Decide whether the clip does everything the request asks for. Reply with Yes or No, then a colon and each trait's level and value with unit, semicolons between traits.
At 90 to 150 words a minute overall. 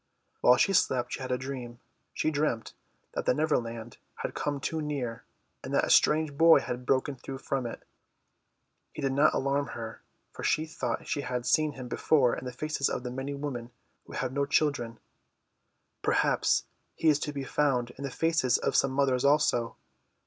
No: average, 185 wpm